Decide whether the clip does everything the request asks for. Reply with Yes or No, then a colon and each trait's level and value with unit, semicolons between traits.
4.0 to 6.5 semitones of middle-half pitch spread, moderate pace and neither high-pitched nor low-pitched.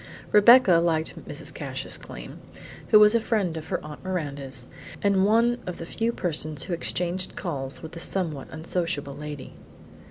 Yes: average, 5.0 semitones; average, 160 wpm; medium, 170 Hz